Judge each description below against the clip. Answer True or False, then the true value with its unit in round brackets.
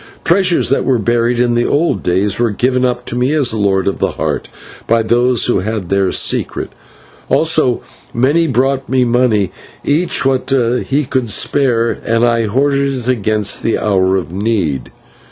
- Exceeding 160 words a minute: True (170 wpm)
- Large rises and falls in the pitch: False (3.9 semitones)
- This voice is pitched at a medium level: False (120 Hz)